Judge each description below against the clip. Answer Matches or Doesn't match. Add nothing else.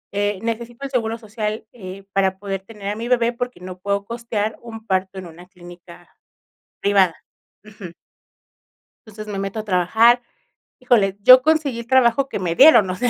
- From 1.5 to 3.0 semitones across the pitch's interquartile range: Doesn't match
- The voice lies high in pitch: Matches